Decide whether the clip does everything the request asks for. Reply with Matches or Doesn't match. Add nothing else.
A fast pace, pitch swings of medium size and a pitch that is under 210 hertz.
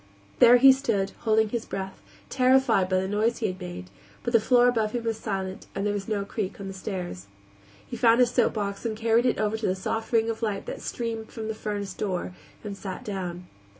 Doesn't match